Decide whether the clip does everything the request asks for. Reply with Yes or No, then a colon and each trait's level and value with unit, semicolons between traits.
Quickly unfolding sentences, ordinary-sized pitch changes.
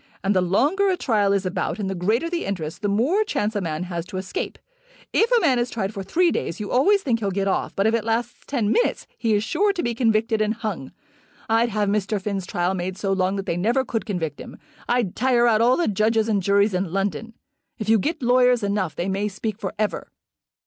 Yes: fast, 240 wpm; average, 3.7 semitones